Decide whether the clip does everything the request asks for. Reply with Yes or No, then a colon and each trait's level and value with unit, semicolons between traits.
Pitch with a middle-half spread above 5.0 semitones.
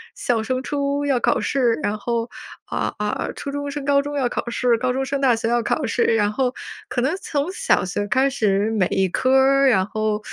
No: average, 4.0 semitones